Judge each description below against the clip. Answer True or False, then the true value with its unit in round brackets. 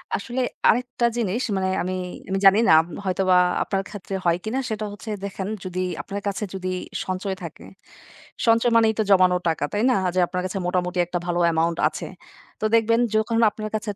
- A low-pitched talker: False (195 Hz)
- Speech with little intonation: False (3.1 semitones)